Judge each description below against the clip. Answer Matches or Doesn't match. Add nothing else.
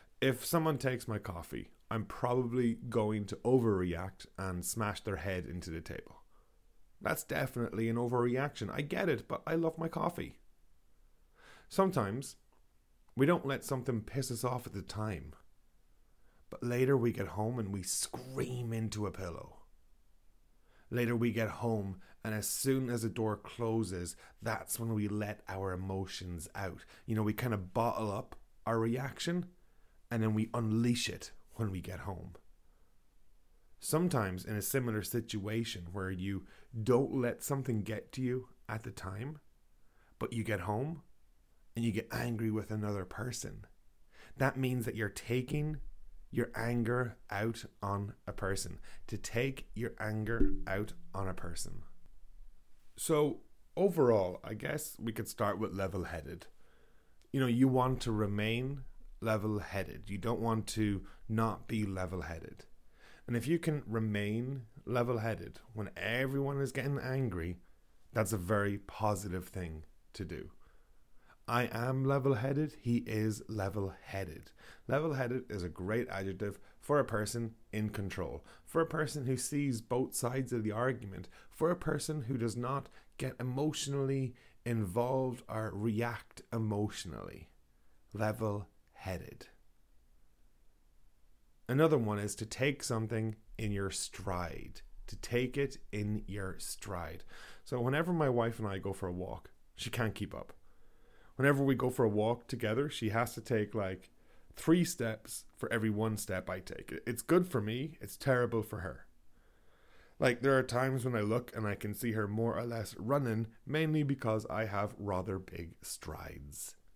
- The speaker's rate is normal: Matches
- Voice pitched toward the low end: Matches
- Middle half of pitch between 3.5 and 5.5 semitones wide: Matches